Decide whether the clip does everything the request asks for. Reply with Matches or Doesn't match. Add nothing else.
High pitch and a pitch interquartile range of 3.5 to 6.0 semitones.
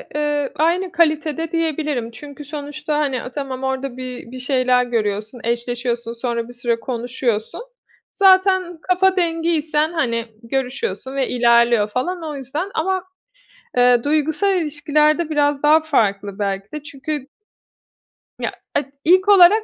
Matches